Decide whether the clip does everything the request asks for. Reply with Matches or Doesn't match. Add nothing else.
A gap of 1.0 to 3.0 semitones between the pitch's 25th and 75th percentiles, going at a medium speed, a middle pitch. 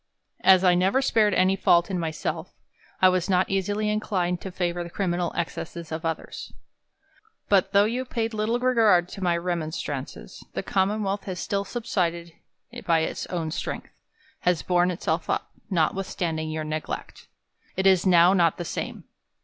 Matches